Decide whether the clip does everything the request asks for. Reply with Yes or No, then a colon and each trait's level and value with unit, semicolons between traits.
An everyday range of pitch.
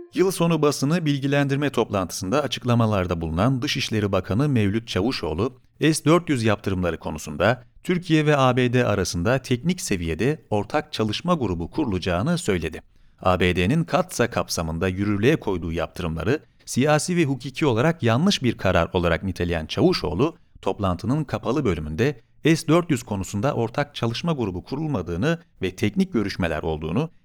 No: wide, 7.6 semitones